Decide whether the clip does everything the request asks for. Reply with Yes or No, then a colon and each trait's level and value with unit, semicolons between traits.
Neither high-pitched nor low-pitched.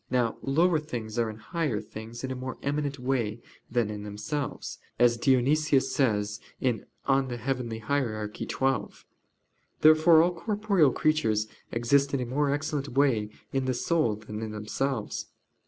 No: low, 130 Hz